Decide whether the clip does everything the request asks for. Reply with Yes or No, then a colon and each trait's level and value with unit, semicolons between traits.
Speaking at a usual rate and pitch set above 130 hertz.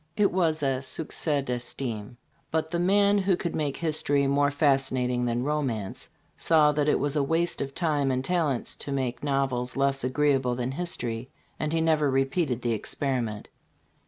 Yes: average, 170 wpm; medium, 140 Hz